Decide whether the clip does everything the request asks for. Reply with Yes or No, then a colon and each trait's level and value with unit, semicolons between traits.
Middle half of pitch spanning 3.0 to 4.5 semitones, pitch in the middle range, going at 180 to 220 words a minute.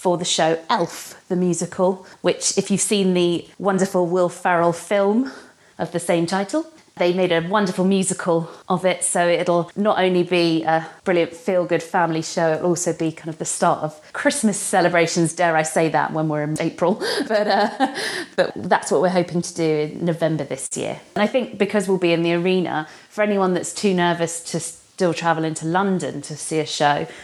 No: narrow, 2.4 semitones; medium, 175 Hz; average, 200 wpm